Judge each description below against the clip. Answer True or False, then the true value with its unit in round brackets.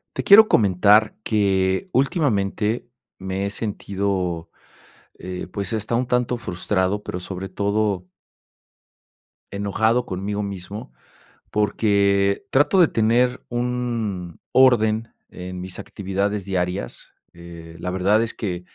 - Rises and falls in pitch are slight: False (3.3 semitones)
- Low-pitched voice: True (100 Hz)